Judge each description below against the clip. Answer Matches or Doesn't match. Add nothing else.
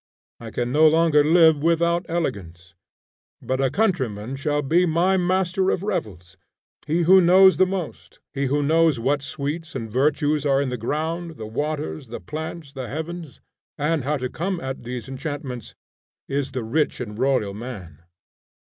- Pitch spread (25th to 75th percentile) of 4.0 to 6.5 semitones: Matches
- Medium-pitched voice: Matches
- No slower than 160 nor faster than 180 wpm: Matches